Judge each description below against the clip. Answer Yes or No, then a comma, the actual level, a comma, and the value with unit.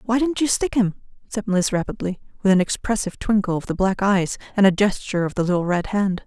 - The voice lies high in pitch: Yes, high, 195 Hz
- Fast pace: Yes, fast, 230 wpm